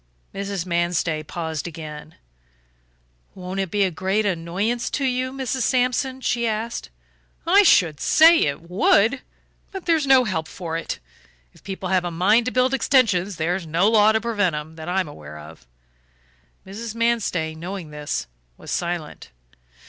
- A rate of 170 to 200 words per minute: No, average, 155 wpm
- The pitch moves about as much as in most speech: No, wide, 6.2 semitones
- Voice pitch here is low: No, high, 190 Hz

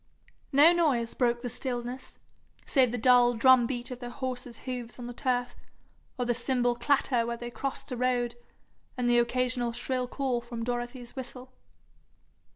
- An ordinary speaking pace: Yes, average, 165 wpm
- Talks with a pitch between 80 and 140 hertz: No, high, 245 Hz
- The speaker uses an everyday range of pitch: No, narrow, 1.1 semitones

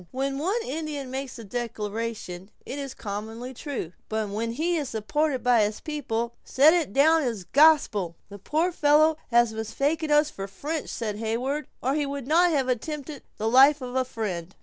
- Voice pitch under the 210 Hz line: No, very high, 260 Hz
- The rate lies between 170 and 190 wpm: Yes, average, 180 wpm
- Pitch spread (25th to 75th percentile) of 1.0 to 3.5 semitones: No, average, 5.2 semitones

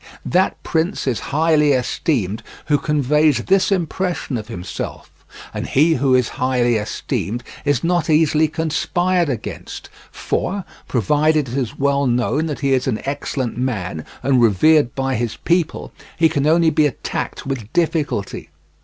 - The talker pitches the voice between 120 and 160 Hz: Yes, medium, 140 Hz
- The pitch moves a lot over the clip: No, average, 4.4 semitones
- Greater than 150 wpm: No, average, 145 wpm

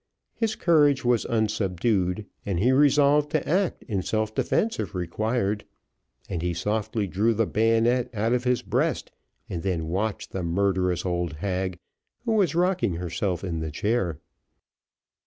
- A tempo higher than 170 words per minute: No, average, 150 wpm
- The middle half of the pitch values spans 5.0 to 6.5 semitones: Yes, wide, 5.4 semitones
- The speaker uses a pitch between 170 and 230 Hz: No, low, 110 Hz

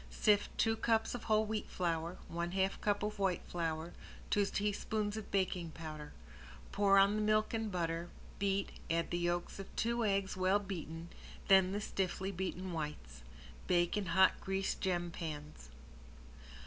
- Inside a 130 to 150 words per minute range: No, average, 160 wpm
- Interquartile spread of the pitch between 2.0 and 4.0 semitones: Yes, average, 3.2 semitones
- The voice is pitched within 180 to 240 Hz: Yes, high, 190 Hz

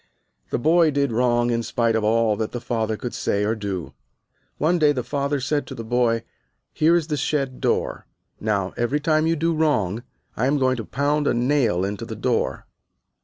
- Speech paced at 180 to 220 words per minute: Yes, average, 200 wpm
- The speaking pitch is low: Yes, low, 125 Hz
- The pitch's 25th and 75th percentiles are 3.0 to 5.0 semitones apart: Yes, average, 4.7 semitones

